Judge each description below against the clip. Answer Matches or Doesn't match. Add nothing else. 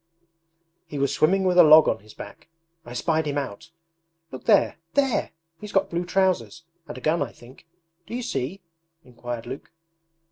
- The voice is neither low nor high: Matches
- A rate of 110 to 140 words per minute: Doesn't match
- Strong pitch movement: Matches